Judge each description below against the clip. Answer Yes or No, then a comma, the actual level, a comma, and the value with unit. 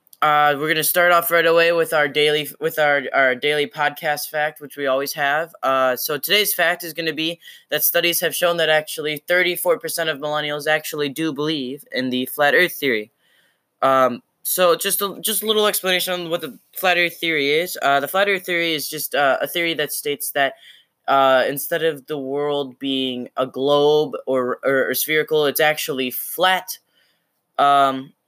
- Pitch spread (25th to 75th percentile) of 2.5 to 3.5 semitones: Yes, average, 3.1 semitones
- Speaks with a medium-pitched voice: Yes, medium, 150 Hz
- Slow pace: No, average, 190 wpm